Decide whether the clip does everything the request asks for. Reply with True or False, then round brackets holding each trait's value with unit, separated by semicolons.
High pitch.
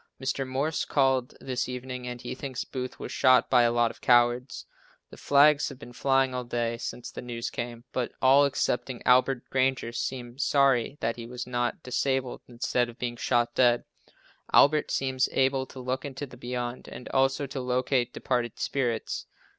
False (125 Hz)